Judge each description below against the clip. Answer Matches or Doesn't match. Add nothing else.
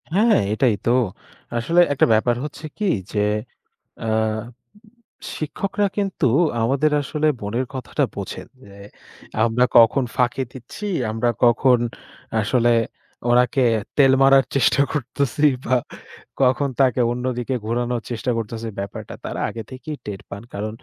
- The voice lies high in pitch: Doesn't match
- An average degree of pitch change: Matches